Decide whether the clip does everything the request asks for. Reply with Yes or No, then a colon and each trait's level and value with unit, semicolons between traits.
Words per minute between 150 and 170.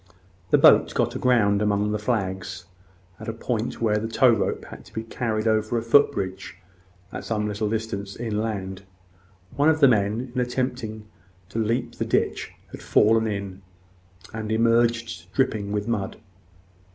Yes: average, 160 wpm